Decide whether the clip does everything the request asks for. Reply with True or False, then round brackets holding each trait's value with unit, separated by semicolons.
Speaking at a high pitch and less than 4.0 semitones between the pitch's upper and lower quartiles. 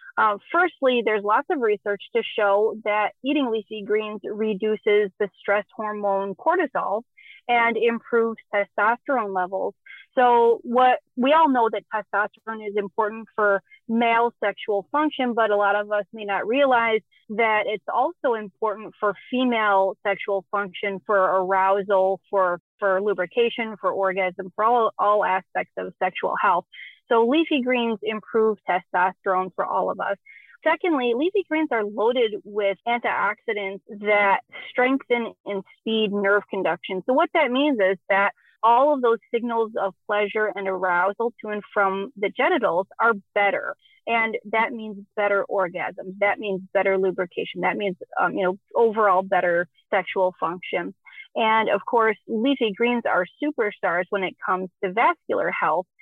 True (215 Hz; 3.3 semitones)